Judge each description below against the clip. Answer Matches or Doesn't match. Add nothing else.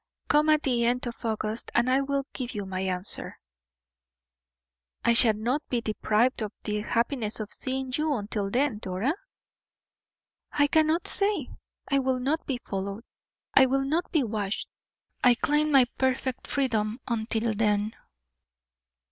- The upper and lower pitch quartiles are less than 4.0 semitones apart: Doesn't match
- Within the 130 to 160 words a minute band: Matches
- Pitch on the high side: Matches